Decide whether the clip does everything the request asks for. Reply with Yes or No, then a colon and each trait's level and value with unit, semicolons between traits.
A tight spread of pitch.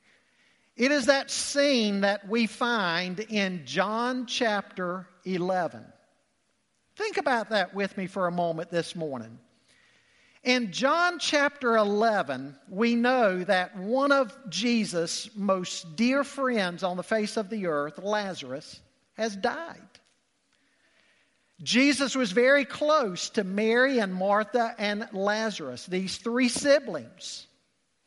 No: average, 5.1 semitones